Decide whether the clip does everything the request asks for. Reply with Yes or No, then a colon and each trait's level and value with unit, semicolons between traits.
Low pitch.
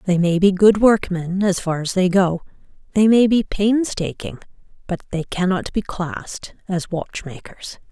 No: high, 190 Hz